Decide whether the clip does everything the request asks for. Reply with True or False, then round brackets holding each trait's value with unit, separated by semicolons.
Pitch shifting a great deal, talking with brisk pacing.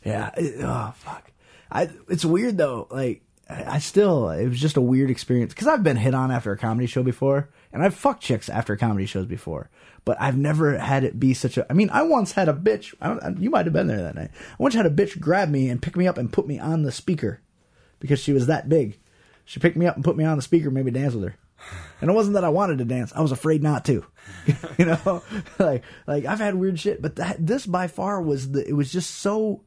True (5.9 semitones; 260 wpm)